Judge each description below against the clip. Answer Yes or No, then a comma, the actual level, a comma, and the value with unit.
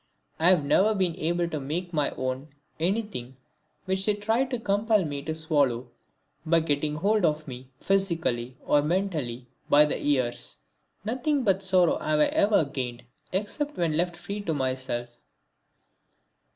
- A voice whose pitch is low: No, medium, 165 Hz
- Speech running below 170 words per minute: Yes, average, 150 wpm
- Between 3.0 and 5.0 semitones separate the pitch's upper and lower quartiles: No, wide, 5.6 semitones